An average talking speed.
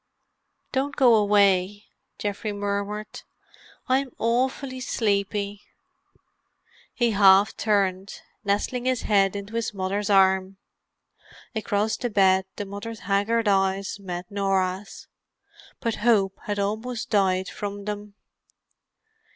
No: slow, 105 wpm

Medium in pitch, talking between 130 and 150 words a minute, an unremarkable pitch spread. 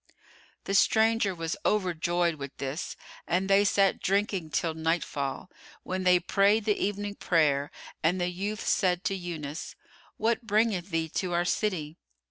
Yes: medium, 180 Hz; average, 145 wpm; average, 3.6 semitones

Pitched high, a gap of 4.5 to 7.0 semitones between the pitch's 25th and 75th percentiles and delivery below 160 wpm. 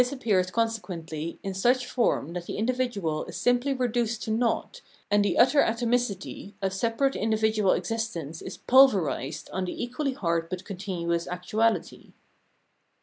Yes: high, 215 Hz; average, 5.2 semitones; average, 145 wpm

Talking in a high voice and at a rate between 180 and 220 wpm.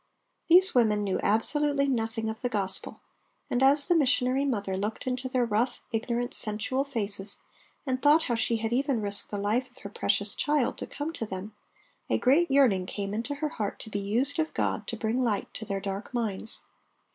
Yes: high, 235 Hz; average, 195 wpm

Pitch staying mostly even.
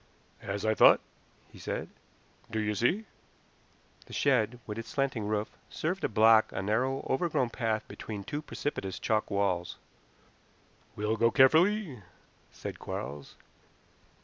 No: average, 4.1 semitones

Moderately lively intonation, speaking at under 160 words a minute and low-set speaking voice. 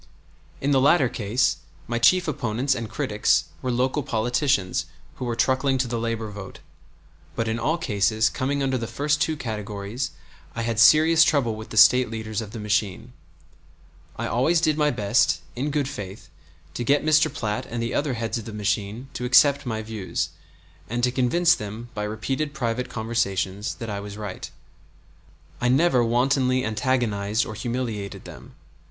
No: average, 3.6 semitones; average, 170 wpm; low, 120 Hz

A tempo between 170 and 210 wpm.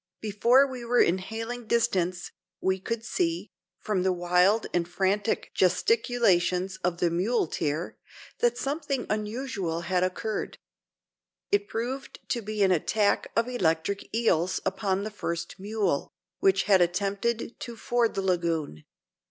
No: slow, 135 wpm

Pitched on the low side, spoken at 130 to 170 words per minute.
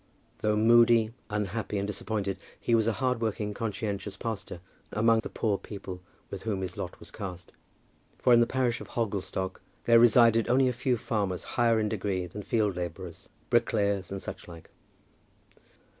Yes: low, 105 Hz; average, 165 wpm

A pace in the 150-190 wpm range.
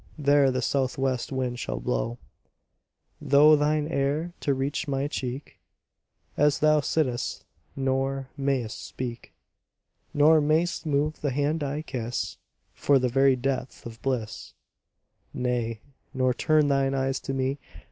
No: slow, 135 wpm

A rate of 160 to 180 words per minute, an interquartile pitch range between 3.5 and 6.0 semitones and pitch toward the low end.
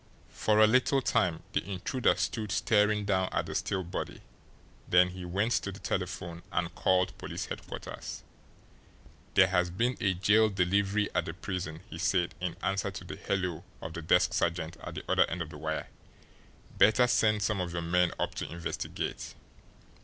No: average, 175 wpm; average, 3.1 semitones; very low, 95 Hz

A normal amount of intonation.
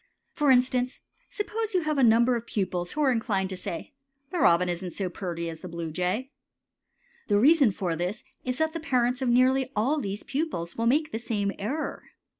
No: wide, 6.7 semitones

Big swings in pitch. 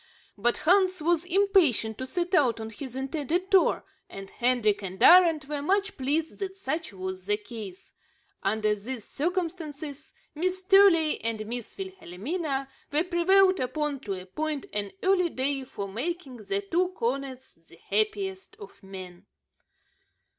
Yes: wide, 8.3 semitones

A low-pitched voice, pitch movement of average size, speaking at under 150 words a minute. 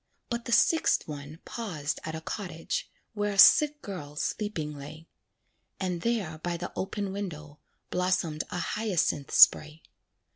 No: medium, 175 Hz; average, 5.0 semitones; average, 140 wpm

